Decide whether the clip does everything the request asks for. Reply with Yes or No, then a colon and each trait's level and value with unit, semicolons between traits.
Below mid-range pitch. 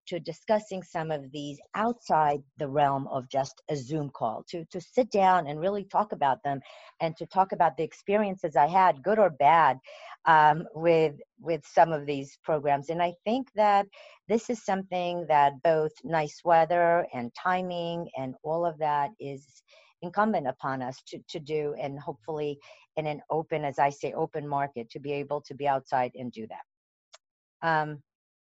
No: medium, 155 Hz